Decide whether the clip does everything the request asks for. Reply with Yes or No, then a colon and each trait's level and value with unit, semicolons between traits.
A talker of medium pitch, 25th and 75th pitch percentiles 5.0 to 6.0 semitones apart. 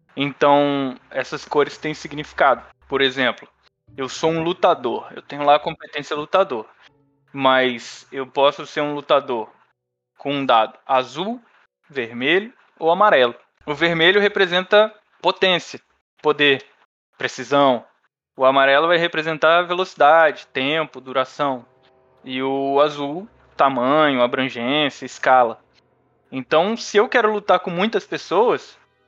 No: medium, 145 Hz; average, 4.4 semitones